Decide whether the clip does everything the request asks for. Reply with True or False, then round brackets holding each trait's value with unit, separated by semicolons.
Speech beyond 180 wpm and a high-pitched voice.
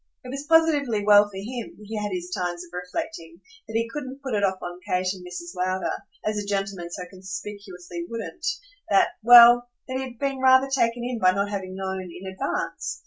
True (200 wpm; 205 Hz)